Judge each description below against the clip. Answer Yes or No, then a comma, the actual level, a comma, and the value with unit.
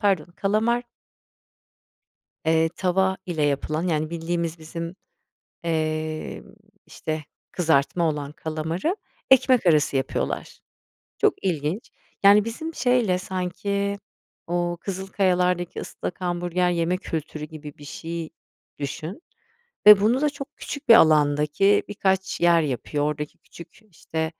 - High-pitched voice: No, medium, 175 Hz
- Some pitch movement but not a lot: Yes, average, 3.9 semitones